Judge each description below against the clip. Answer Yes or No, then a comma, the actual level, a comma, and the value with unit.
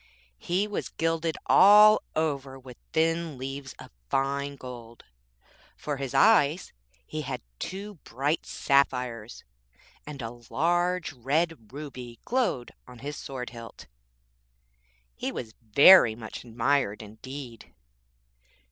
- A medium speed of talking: No, slow, 110 wpm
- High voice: No, medium, 140 Hz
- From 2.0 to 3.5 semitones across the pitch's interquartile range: No, average, 5.1 semitones